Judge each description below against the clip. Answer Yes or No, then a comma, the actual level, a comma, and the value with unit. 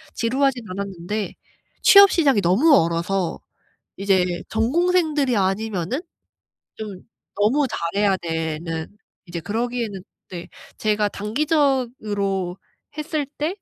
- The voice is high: Yes, high, 210 Hz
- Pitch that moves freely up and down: Yes, wide, 6.5 semitones